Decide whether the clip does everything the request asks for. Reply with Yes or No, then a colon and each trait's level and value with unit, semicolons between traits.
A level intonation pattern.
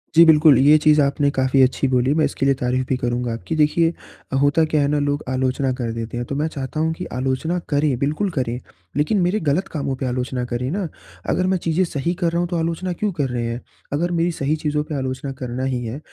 No: average, 3.8 semitones